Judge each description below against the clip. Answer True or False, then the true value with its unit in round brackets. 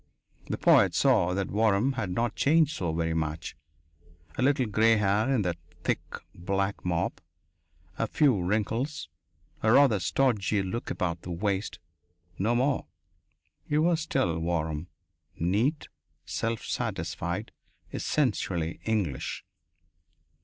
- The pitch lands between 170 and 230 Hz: False (105 Hz)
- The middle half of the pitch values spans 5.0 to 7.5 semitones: True (5.6 semitones)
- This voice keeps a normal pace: False (120 wpm)